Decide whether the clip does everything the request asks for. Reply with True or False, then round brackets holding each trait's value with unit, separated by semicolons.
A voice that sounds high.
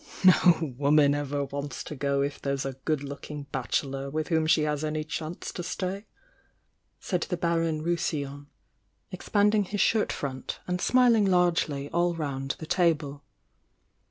False (155 Hz)